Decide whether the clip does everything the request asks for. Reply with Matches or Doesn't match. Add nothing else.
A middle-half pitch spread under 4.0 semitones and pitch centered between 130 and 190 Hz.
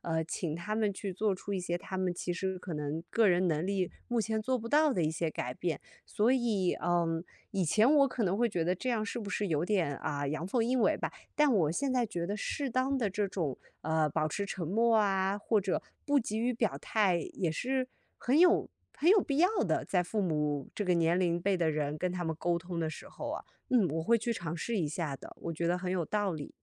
Doesn't match